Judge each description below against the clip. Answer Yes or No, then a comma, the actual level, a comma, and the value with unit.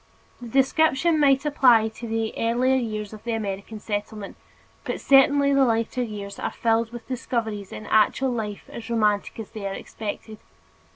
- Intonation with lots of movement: No, average, 3.4 semitones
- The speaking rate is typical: Yes, average, 165 wpm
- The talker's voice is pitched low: No, high, 225 Hz